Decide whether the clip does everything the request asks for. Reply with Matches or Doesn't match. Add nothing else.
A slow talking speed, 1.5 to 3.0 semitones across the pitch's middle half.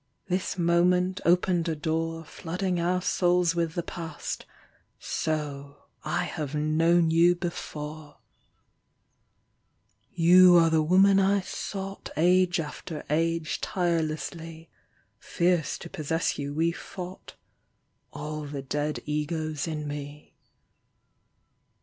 Matches